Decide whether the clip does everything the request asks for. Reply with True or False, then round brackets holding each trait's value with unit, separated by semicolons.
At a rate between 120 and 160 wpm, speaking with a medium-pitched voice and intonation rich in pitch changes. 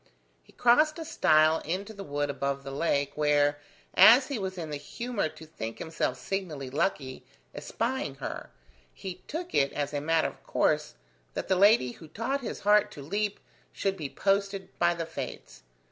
False (175 wpm; 165 Hz; 6.0 semitones)